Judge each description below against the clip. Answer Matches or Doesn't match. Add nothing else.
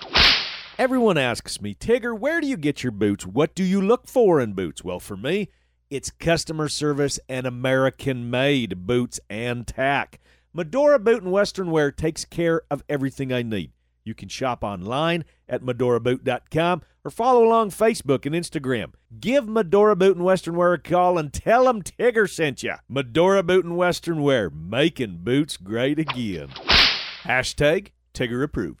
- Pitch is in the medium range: Matches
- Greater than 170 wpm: Doesn't match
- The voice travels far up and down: Matches